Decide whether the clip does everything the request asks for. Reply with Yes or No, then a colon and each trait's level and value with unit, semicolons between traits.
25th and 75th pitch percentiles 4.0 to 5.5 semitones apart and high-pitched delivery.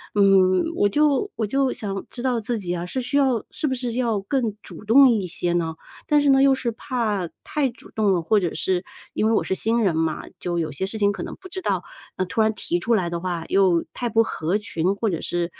Yes: average, 5.2 semitones; high, 210 Hz